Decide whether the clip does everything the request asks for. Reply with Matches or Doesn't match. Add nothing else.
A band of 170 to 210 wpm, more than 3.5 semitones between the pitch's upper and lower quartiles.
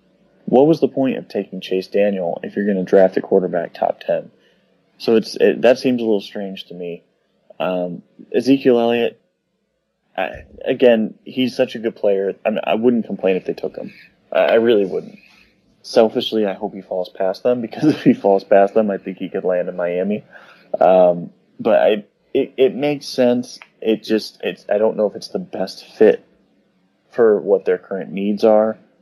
Matches